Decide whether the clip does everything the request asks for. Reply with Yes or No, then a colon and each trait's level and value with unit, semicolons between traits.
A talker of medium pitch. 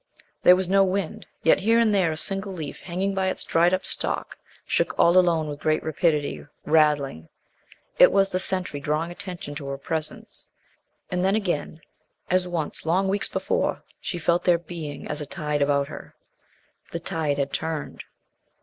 Yes: medium, 170 Hz